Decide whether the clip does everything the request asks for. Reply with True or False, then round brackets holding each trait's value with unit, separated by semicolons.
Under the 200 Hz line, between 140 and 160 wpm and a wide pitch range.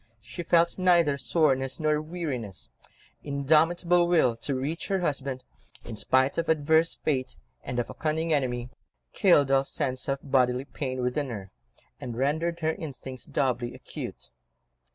False (140 Hz; 145 wpm; 3.9 semitones)